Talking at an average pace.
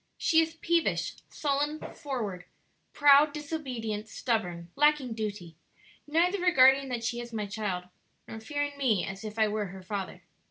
Yes: average, 150 wpm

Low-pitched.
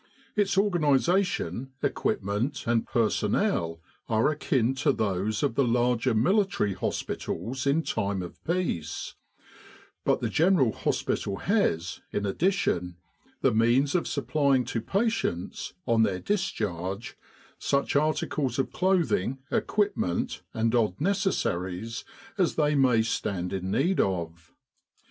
Yes: low, 120 Hz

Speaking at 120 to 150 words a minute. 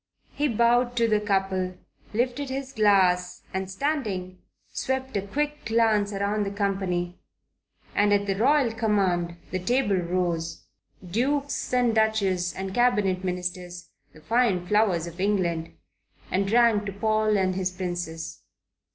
Yes: slow, 135 wpm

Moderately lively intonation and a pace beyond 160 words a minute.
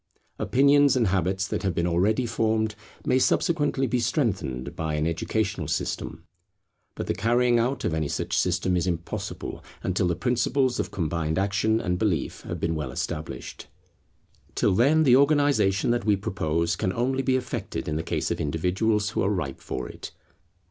No: wide, 6.5 semitones; average, 170 wpm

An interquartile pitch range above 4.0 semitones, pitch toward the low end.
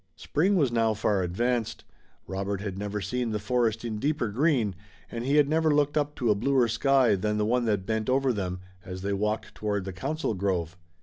Yes: average, 4.7 semitones; low, 110 Hz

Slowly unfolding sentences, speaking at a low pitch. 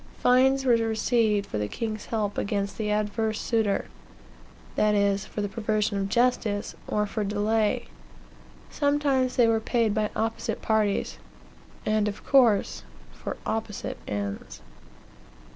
No: slow, 125 wpm; high, 215 Hz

